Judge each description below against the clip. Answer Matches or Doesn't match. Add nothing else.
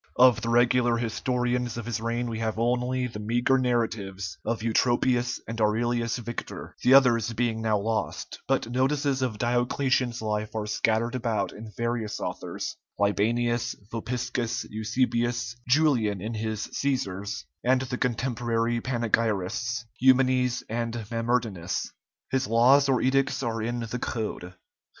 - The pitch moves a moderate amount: Doesn't match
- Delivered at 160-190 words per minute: Doesn't match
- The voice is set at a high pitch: Doesn't match